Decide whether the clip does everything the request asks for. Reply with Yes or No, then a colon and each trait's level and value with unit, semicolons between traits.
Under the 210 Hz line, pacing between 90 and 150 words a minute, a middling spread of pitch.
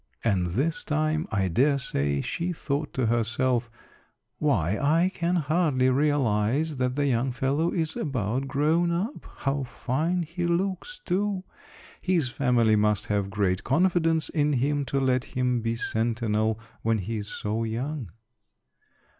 No: low, 135 Hz; average, 145 wpm; wide, 5.7 semitones